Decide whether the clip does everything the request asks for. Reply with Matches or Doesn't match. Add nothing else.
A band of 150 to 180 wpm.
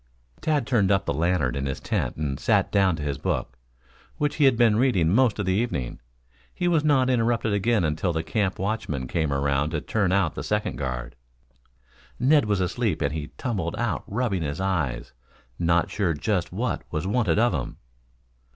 Doesn't match